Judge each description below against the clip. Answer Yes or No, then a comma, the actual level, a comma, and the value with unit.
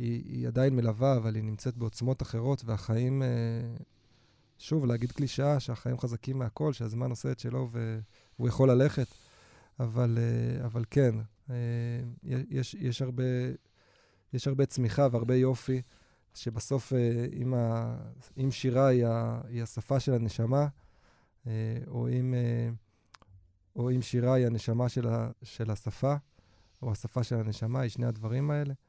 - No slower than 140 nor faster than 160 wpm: No, average, 120 wpm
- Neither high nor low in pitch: No, low, 120 Hz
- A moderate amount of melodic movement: No, narrow, 2.2 semitones